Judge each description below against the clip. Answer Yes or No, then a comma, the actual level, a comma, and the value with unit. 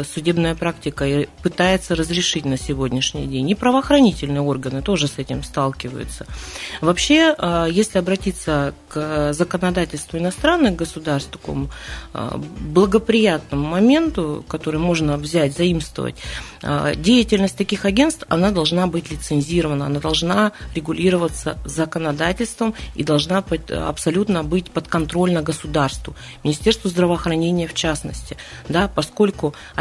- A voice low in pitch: No, medium, 170 Hz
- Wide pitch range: No, average, 4.1 semitones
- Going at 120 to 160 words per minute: No, slow, 110 wpm